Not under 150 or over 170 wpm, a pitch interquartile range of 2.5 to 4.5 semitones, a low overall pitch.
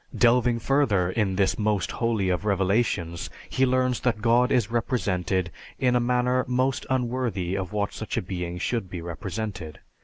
No: average, 160 wpm; average, 5.0 semitones; low, 110 Hz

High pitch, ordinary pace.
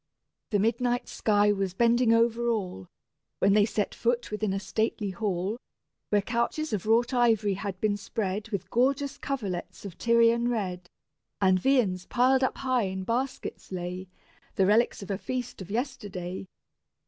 Yes: high, 215 Hz; average, 155 wpm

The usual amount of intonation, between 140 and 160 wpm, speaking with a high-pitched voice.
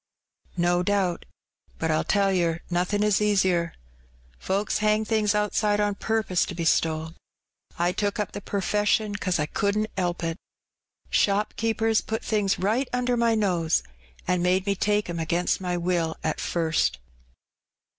Yes: average, 3.3 semitones; average, 155 wpm; high, 195 Hz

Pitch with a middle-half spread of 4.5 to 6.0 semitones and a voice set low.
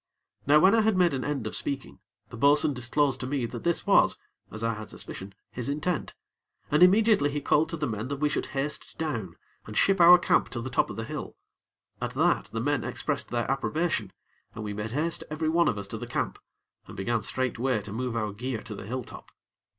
Yes: average, 5.1 semitones; low, 130 Hz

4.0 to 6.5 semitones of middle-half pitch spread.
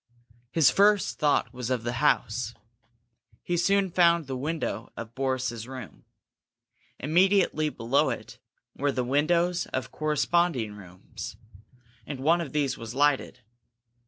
Yes: wide, 5.5 semitones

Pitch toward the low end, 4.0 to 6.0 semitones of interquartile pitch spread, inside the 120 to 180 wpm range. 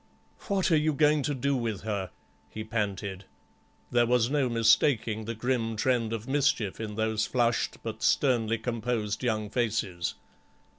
No: low, 115 Hz; average, 2.8 semitones; average, 150 wpm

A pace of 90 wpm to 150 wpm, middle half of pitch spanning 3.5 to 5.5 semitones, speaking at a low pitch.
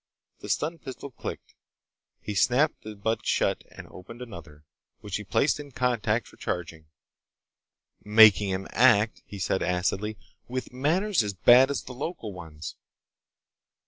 Yes: average, 145 wpm; average, 4.9 semitones; low, 110 Hz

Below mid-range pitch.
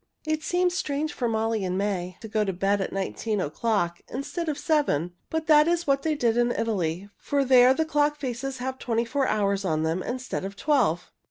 No: high, 240 Hz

